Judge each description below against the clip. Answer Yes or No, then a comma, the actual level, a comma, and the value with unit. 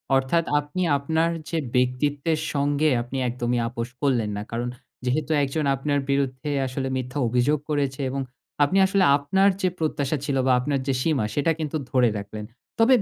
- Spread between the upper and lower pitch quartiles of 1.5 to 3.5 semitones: Yes, average, 3.2 semitones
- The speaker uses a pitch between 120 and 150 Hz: Yes, medium, 140 Hz